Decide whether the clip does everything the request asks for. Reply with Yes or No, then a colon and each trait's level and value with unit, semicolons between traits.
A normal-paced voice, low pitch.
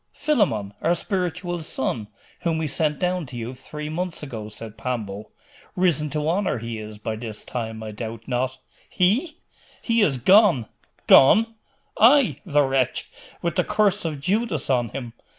No: average, 160 wpm; medium, 150 Hz